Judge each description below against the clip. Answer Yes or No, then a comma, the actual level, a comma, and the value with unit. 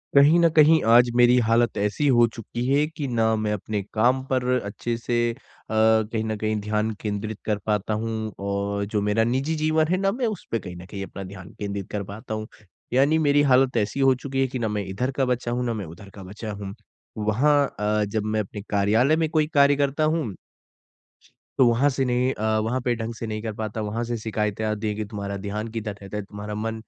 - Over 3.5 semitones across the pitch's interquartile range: Yes, average, 3.9 semitones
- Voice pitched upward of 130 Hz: No, low, 110 Hz